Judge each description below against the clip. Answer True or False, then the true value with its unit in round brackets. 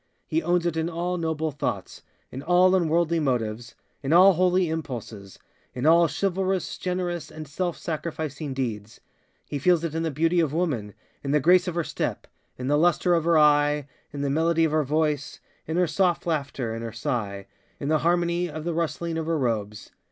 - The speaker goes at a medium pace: True (170 wpm)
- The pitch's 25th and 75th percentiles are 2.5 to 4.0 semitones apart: True (3.6 semitones)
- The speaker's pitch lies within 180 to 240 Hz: False (160 Hz)